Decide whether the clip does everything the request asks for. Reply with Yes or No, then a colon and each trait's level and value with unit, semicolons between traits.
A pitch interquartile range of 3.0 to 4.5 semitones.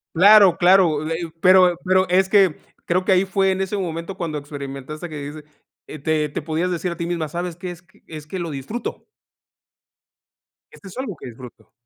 Yes: average, 3.5 semitones